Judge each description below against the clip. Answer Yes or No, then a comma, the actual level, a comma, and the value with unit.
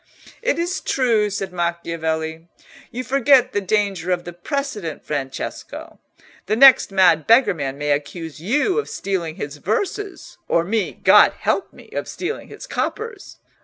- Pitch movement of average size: No, wide, 8.5 semitones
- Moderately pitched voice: No, high, 195 Hz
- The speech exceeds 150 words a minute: No, average, 145 wpm